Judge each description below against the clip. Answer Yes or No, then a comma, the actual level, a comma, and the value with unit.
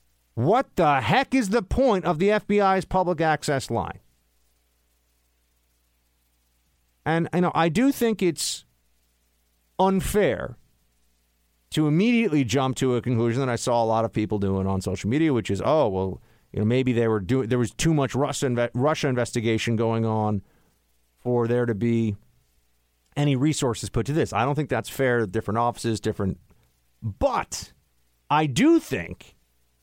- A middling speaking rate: Yes, average, 160 wpm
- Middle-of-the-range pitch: No, low, 115 Hz